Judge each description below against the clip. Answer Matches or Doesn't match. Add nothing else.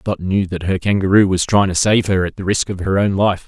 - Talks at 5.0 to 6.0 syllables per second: Matches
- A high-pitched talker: Doesn't match